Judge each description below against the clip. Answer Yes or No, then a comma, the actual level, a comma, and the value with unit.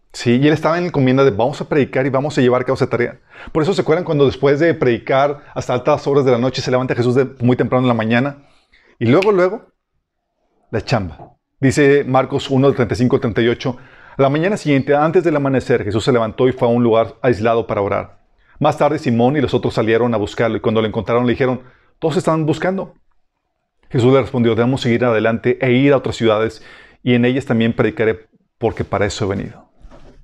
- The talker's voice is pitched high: No, low, 130 Hz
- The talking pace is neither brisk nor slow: No, fast, 210 wpm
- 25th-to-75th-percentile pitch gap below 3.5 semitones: Yes, average, 3.1 semitones